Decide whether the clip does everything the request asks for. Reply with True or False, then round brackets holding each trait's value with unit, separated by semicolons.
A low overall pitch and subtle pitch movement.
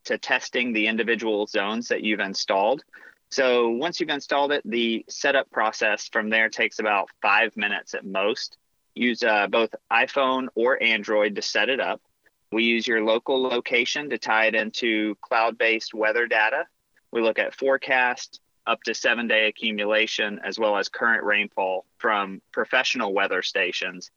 True (115 Hz; 2.3 semitones)